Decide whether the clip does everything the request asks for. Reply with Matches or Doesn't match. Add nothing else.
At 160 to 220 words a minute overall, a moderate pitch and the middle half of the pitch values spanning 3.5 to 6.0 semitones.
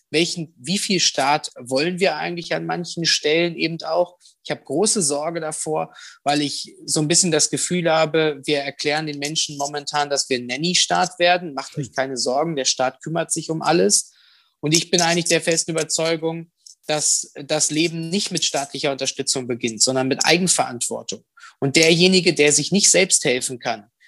Doesn't match